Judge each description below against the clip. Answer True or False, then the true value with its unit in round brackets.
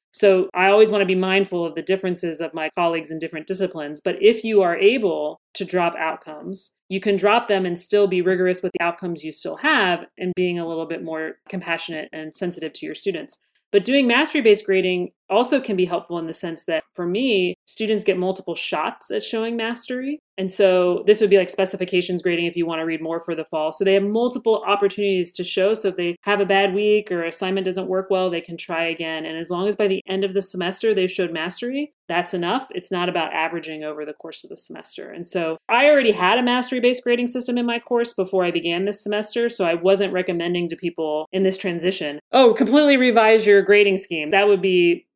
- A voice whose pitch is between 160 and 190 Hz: True (185 Hz)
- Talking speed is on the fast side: True (230 wpm)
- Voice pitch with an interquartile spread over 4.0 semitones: False (3.3 semitones)